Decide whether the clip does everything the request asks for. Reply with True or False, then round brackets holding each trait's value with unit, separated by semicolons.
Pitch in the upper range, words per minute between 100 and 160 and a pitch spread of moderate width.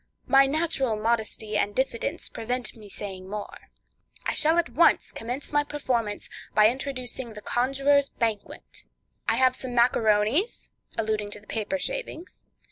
True (240 Hz; 140 wpm; 4.4 semitones)